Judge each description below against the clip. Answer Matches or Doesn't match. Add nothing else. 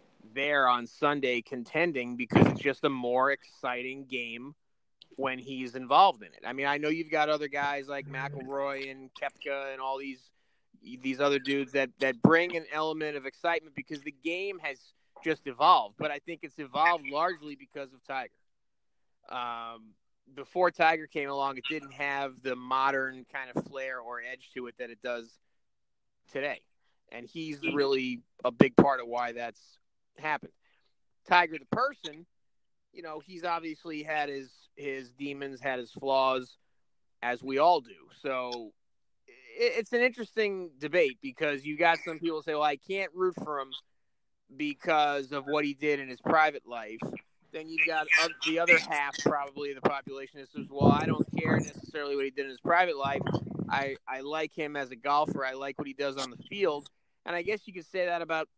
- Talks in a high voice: Doesn't match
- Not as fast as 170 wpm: Doesn't match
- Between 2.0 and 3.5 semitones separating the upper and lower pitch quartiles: Matches